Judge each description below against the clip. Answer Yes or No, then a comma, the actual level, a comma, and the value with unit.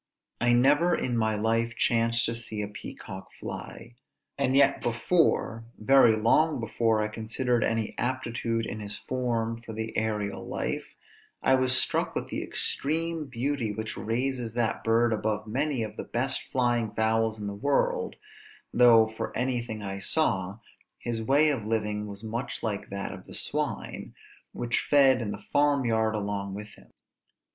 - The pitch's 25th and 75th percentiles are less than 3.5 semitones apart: Yes, average, 2.9 semitones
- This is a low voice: Yes, low, 115 Hz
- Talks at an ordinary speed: Yes, average, 160 wpm